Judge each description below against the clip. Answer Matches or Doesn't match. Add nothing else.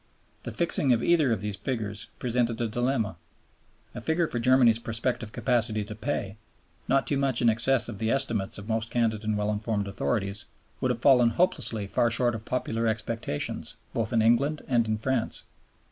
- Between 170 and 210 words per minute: Matches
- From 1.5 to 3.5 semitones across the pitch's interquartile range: Matches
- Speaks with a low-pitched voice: Matches